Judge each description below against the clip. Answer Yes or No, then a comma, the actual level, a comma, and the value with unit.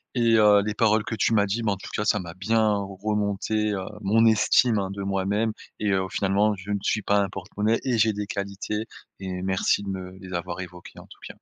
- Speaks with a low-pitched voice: Yes, low, 100 Hz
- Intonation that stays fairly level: Yes, narrow, 1.9 semitones